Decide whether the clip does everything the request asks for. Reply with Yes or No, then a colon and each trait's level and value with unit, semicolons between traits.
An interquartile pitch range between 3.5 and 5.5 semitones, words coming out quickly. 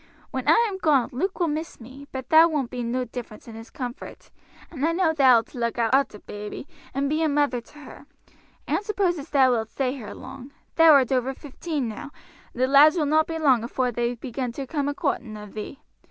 Yes: average, 4.1 semitones; fast, 225 wpm